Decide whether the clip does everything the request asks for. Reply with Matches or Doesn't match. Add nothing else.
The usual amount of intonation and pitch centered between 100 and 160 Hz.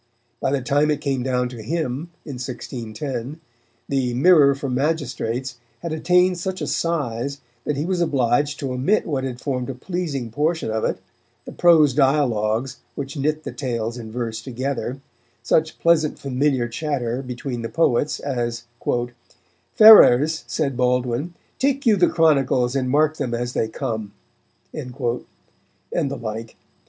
Matches